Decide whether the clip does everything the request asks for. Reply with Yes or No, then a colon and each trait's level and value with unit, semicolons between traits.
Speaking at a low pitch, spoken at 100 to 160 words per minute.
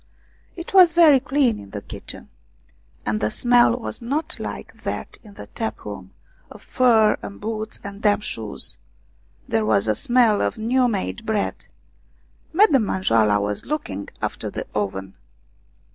No: high, 215 Hz; average, 150 wpm